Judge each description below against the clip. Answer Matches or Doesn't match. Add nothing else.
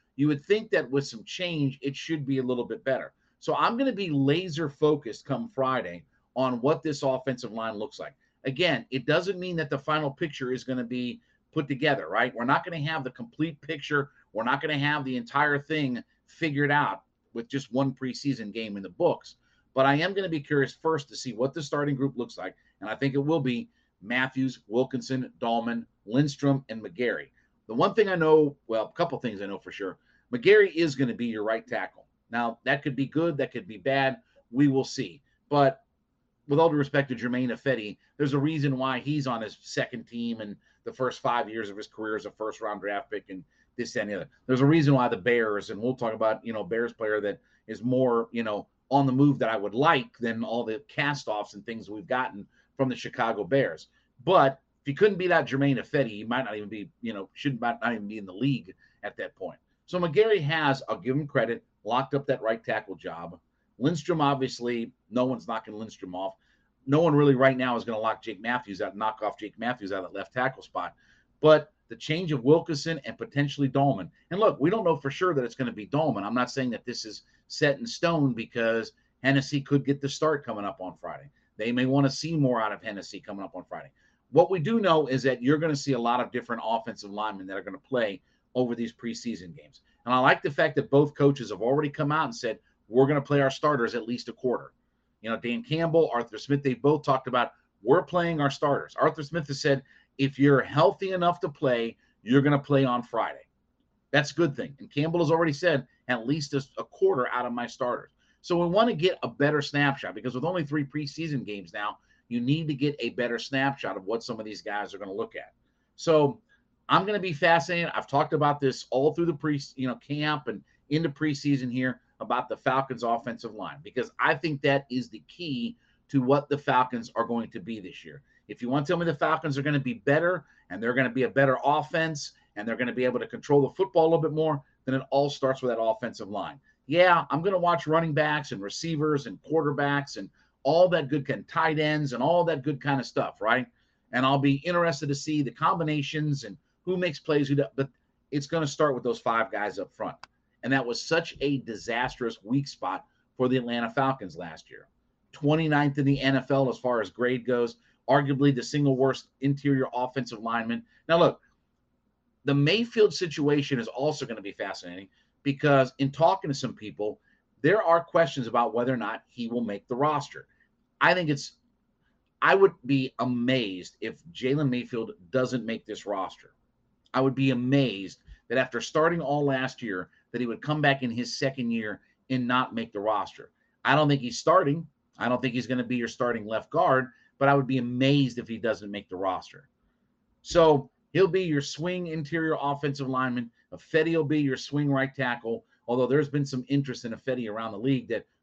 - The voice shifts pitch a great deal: Doesn't match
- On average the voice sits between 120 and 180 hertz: Matches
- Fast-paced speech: Matches